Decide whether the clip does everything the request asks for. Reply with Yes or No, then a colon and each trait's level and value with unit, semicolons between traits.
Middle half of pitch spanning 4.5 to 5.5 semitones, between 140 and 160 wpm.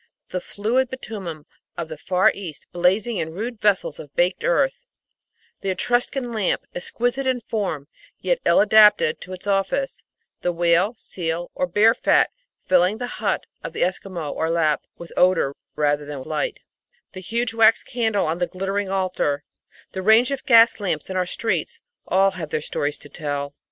No: average, 5.2 semitones; average, 170 wpm